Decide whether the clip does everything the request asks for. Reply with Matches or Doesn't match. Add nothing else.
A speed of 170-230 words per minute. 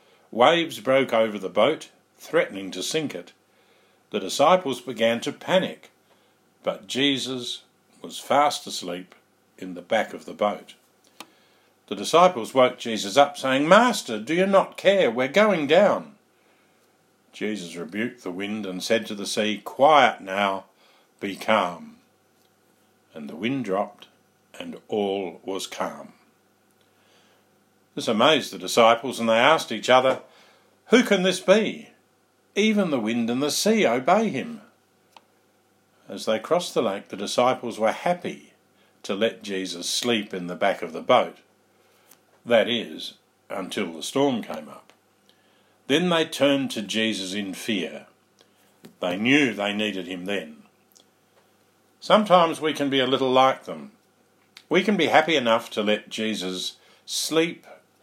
Doesn't match